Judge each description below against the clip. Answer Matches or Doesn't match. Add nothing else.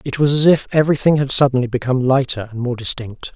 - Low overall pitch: Matches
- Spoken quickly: Matches